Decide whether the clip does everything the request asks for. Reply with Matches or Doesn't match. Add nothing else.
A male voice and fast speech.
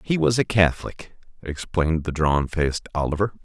Doesn't match